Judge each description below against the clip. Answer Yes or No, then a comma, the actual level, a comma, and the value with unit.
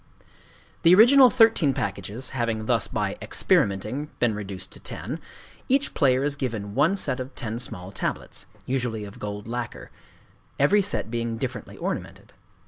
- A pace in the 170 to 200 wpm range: No, slow, 135 wpm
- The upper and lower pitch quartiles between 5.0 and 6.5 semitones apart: Yes, average, 5.3 semitones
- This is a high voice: No, low, 125 Hz